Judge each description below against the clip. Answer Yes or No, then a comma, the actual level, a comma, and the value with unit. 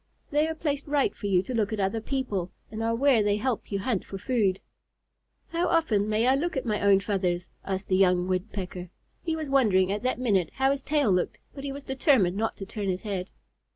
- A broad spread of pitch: Yes, wide, 5.8 semitones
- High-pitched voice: Yes, high, 215 Hz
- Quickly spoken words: Yes, fast, 225 wpm